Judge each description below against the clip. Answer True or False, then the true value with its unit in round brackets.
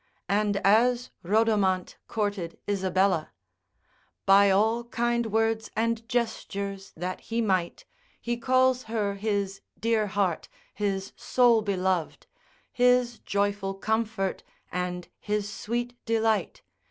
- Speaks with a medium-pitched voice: False (210 Hz)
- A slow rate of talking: True (105 wpm)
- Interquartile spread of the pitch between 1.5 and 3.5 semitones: True (3.0 semitones)